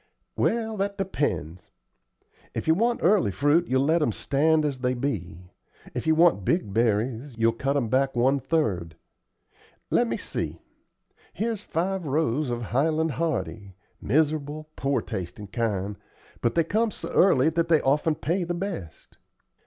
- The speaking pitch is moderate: Yes, medium, 145 Hz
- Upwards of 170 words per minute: No, average, 155 wpm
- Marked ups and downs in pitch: Yes, wide, 6.4 semitones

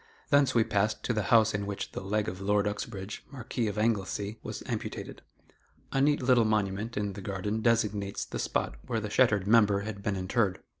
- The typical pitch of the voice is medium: No, low, 105 Hz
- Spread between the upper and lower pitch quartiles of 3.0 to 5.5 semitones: No, narrow, 2.4 semitones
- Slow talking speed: No, average, 195 wpm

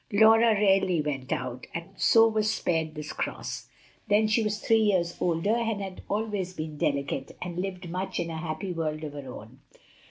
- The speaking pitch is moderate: Yes, medium, 180 Hz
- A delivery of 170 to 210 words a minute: Yes, average, 180 wpm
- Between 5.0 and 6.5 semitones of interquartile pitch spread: Yes, average, 5.3 semitones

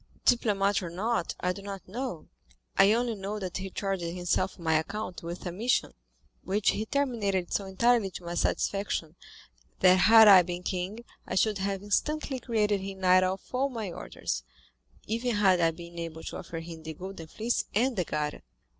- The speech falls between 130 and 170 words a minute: No, average, 180 wpm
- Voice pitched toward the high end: Yes, high, 195 Hz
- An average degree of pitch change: Yes, average, 3.5 semitones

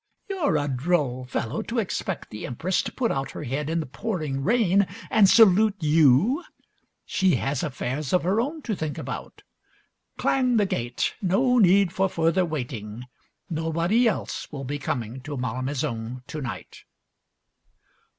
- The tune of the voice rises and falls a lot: Yes, wide, 6.8 semitones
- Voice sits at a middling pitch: Yes, medium, 160 Hz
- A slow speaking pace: No, average, 150 wpm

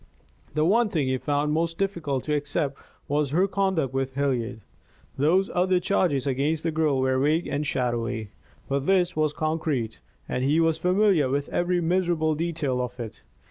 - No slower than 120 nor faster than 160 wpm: No, average, 170 wpm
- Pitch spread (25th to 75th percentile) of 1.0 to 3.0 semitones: No, average, 4.2 semitones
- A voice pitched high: No, medium, 150 Hz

